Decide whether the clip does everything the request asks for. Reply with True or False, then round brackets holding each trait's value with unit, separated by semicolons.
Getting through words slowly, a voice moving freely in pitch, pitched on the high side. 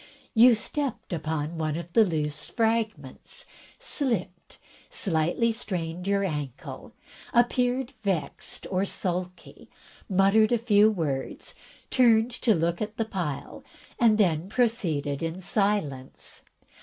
True (115 wpm; 5.7 semitones; 195 Hz)